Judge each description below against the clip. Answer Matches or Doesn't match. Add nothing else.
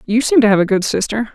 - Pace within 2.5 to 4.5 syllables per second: Doesn't match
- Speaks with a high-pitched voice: Matches